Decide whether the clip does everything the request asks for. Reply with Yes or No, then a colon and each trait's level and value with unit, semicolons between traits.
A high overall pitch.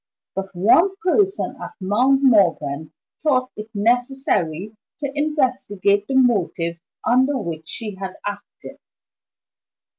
Yes: high, 220 Hz